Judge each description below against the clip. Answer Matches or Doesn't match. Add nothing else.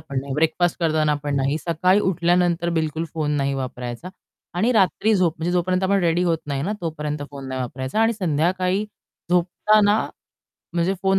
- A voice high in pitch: Doesn't match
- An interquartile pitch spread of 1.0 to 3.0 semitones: Doesn't match